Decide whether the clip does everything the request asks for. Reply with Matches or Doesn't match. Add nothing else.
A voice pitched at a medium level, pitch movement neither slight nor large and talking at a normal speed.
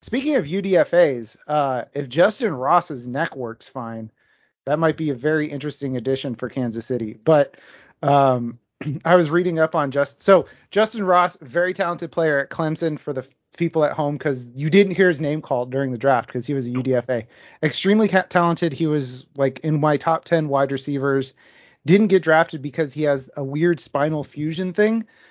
Matches